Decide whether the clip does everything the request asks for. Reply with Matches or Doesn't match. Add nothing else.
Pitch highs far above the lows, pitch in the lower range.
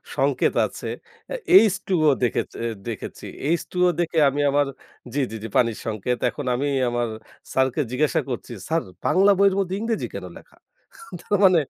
Doesn't match